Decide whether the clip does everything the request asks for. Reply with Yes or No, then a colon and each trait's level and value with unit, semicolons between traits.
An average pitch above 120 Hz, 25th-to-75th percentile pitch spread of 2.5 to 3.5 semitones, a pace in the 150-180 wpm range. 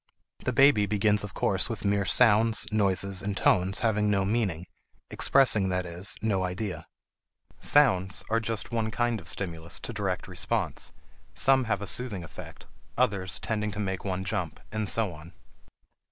No: low, 100 Hz; average, 2.9 semitones; average, 160 wpm